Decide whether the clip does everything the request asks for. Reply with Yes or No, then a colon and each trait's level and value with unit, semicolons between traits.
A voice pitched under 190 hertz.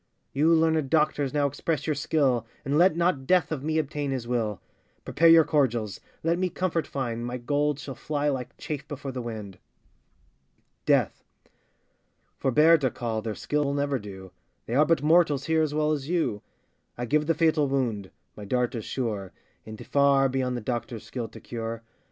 Yes: medium, 140 Hz